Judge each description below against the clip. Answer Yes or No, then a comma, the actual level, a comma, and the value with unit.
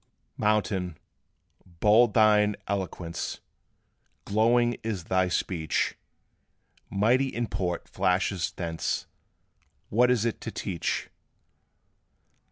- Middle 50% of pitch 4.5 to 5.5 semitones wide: No, average, 3.8 semitones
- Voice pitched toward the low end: Yes, low, 100 Hz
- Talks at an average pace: No, slow, 80 wpm